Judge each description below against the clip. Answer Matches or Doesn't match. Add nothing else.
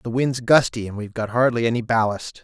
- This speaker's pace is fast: Matches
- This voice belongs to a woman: Doesn't match